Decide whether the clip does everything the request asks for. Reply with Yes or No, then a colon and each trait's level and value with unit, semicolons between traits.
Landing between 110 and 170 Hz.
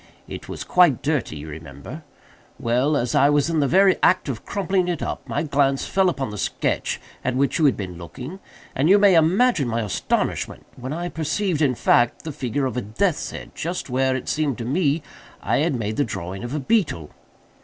Yes: medium, 140 Hz